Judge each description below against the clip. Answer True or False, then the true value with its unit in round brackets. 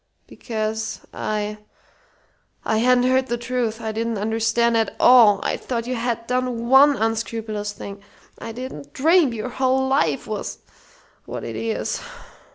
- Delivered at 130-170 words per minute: True (145 wpm)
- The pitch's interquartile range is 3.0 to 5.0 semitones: False (2.5 semitones)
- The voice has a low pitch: False (230 Hz)